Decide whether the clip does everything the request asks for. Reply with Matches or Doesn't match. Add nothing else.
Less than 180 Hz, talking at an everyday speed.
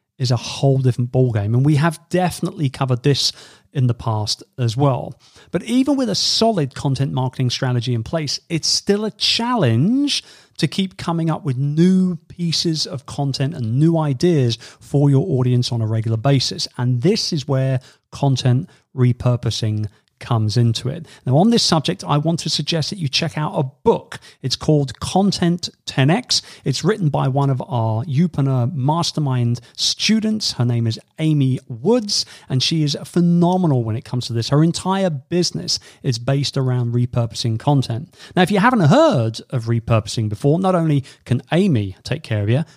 Matches